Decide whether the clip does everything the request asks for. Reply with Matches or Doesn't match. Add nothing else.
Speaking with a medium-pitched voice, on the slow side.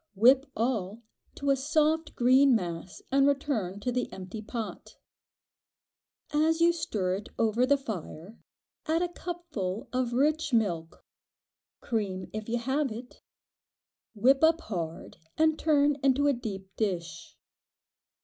Doesn't match